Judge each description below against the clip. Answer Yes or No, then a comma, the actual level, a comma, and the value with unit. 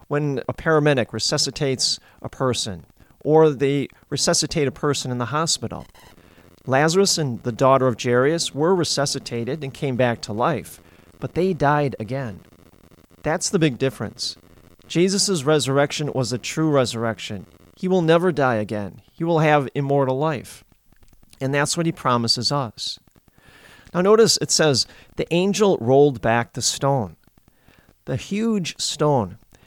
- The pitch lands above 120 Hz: Yes, low, 135 Hz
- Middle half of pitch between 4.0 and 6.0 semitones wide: Yes, average, 5.2 semitones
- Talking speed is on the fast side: No, average, 140 wpm